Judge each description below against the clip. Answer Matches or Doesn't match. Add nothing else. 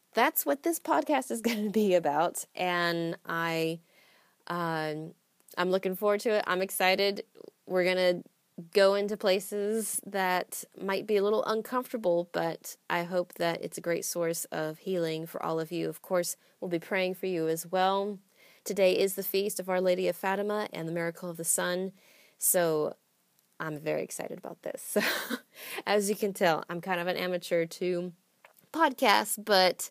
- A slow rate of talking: Doesn't match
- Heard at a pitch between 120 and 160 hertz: Doesn't match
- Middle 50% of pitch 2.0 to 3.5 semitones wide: Matches